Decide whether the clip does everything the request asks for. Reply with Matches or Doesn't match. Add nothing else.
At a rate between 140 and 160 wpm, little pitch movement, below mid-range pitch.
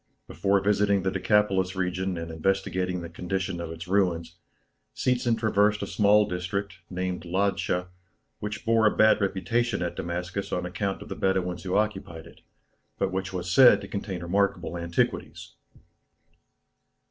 Matches